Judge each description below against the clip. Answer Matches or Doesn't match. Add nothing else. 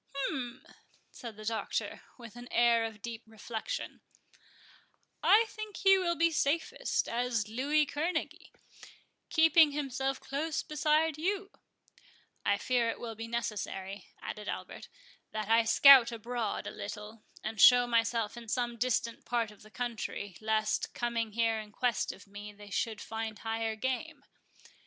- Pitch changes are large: Doesn't match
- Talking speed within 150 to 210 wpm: Doesn't match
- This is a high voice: Matches